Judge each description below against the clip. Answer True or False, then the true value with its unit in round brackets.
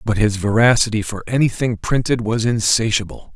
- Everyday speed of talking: True (145 wpm)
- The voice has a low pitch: True (110 Hz)